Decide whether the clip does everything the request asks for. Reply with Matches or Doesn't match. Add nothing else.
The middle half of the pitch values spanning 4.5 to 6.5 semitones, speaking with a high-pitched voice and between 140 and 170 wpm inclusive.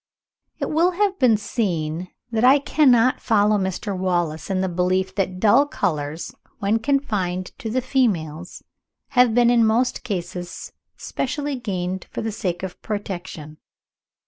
Matches